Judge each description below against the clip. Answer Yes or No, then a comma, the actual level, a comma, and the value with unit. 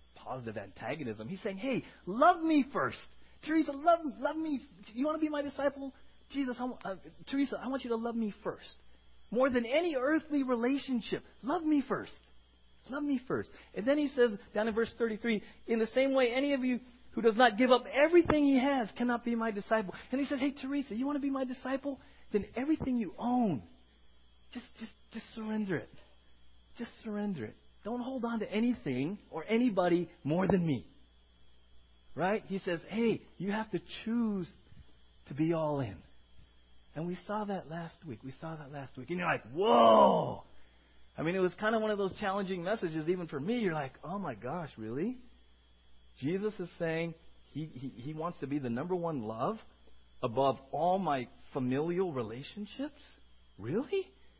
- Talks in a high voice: Yes, high, 200 Hz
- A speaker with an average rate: Yes, average, 185 wpm